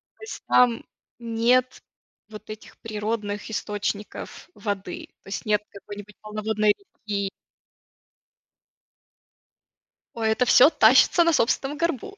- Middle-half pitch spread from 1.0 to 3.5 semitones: Yes, average, 3.2 semitones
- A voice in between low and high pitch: No, high, 220 Hz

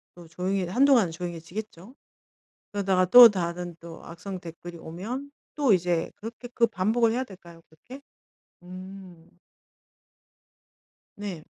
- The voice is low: No, medium, 185 Hz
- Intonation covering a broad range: No, average, 4.6 semitones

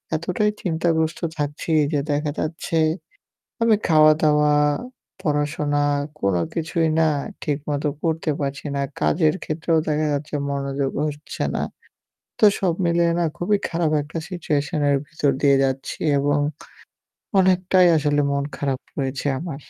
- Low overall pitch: No, medium, 150 Hz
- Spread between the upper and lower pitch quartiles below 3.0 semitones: Yes, narrow, 2.4 semitones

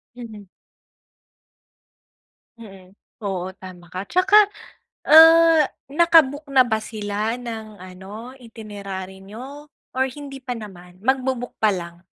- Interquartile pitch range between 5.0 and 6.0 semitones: Yes, wide, 5.6 semitones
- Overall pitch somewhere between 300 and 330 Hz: No, high, 220 Hz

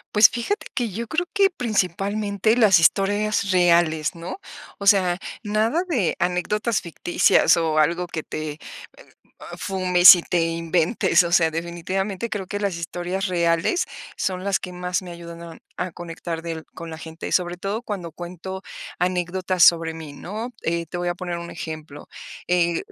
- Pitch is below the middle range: No, medium, 180 Hz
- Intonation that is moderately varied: Yes, average, 3.0 semitones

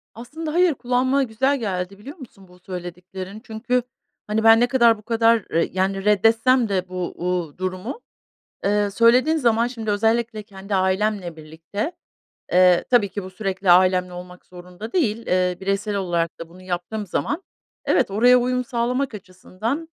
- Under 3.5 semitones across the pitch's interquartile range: No, average, 4.4 semitones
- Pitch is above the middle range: Yes, high, 210 Hz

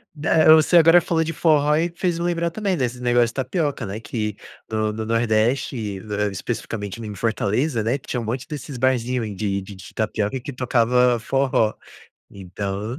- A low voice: Yes, low, 120 Hz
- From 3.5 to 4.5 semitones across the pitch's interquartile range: No, wide, 5.5 semitones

